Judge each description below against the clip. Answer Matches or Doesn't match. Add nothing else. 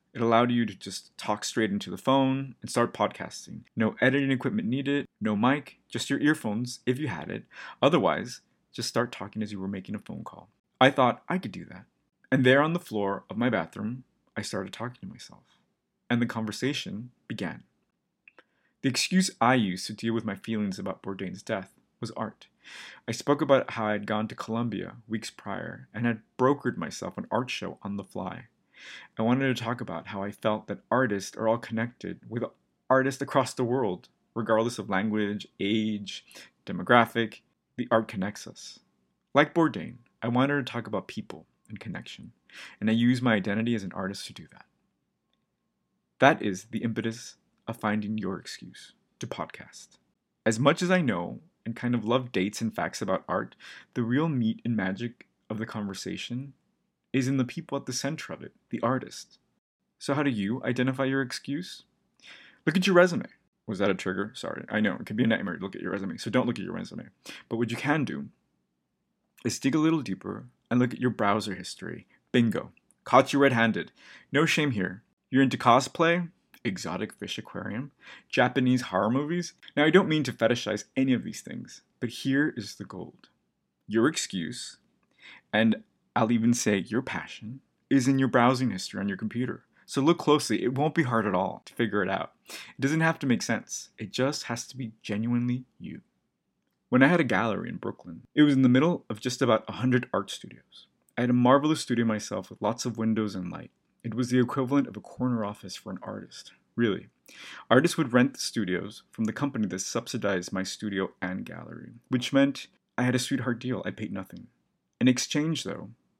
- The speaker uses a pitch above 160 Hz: Doesn't match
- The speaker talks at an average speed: Matches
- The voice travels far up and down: Doesn't match